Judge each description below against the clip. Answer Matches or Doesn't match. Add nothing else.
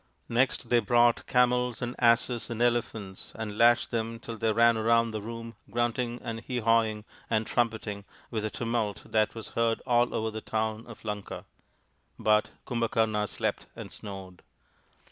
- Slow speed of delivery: Doesn't match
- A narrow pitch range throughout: Matches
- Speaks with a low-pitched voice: Matches